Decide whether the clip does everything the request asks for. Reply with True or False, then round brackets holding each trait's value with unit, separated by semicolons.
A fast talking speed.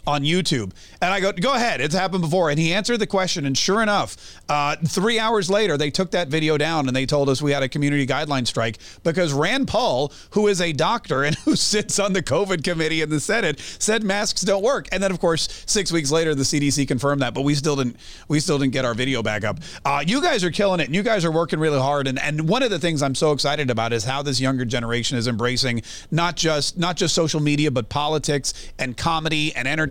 True (245 wpm)